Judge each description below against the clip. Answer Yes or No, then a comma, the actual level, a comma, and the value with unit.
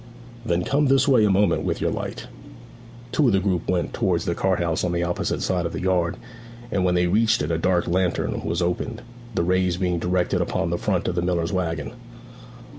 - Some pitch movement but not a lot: No, narrow, 1.8 semitones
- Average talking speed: No, fast, 215 wpm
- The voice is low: Yes, very low, 90 Hz